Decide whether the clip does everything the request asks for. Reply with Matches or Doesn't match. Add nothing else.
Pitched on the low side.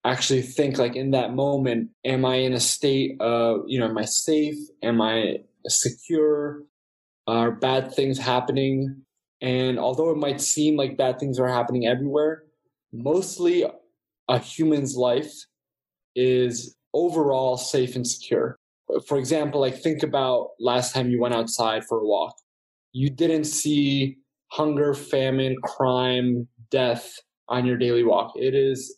Matches